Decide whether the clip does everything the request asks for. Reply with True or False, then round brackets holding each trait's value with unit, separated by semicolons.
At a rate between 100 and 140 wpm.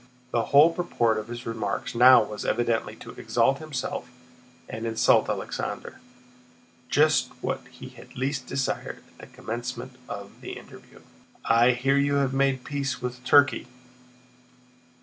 True (135 wpm)